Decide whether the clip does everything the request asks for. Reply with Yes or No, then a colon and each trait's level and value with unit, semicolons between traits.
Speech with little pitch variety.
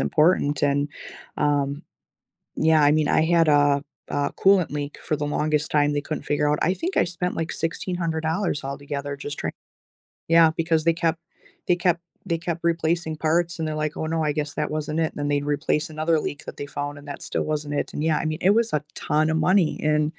Yes: narrow, 2.2 semitones